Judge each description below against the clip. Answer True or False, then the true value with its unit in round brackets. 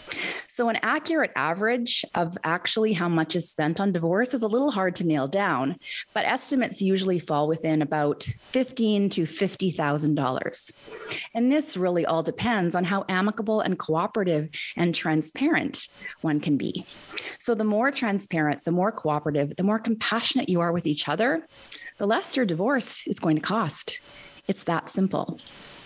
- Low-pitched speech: False (190 Hz)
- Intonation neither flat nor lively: False (6.3 semitones)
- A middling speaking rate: True (160 wpm)